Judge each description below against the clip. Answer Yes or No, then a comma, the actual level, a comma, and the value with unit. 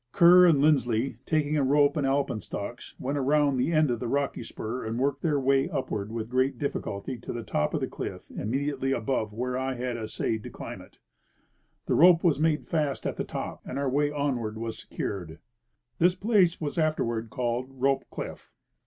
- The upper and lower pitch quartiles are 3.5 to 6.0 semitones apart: Yes, average, 3.9 semitones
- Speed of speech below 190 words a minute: No, average, 195 wpm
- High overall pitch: No, low, 135 Hz